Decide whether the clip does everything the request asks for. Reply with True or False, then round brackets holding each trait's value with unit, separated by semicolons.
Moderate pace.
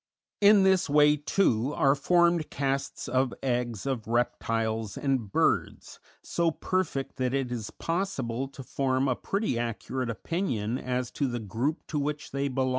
True (155 wpm)